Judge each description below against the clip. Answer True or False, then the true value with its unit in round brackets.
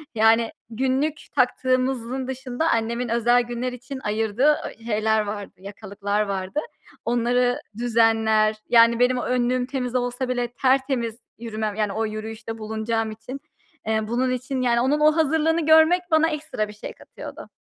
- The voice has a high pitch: True (240 Hz)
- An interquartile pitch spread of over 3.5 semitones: False (2.8 semitones)